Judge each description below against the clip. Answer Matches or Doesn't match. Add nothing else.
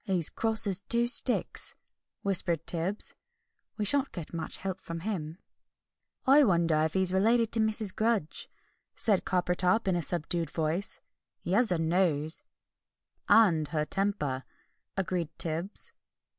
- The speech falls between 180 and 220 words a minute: Doesn't match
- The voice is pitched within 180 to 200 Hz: Matches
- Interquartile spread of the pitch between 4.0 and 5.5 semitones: Matches